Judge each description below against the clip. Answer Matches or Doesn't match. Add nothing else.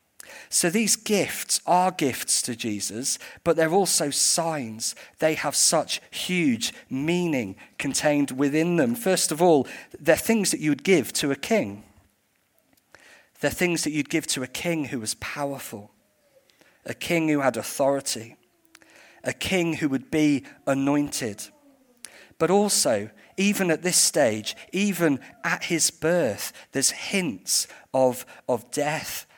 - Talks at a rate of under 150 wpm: Matches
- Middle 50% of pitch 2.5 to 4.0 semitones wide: Doesn't match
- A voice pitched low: Doesn't match